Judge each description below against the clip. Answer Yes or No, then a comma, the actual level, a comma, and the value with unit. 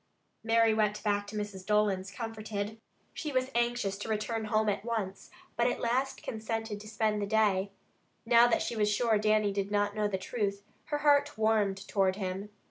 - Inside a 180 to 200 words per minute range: Yes, average, 185 wpm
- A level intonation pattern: Yes, narrow, 1.9 semitones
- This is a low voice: No, high, 215 Hz